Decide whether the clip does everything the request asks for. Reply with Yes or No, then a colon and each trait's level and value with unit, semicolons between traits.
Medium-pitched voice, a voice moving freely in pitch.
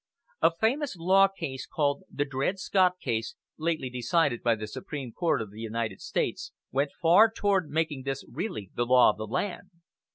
Yes: medium, 145 Hz; wide, 7.2 semitones